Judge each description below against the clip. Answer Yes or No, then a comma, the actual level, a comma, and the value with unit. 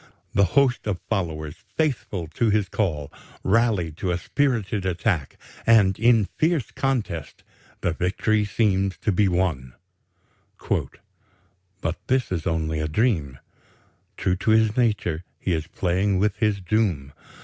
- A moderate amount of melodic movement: Yes, average, 4.7 semitones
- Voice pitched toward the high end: No, very low, 95 Hz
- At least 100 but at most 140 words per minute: Yes, slow, 135 wpm